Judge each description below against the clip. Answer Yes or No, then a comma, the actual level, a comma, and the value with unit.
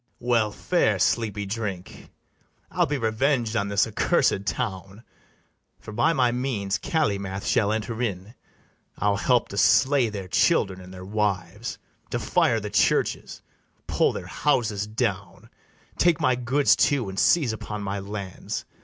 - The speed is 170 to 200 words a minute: No, average, 145 wpm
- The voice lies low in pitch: Yes, low, 105 Hz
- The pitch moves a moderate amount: Yes, average, 3.7 semitones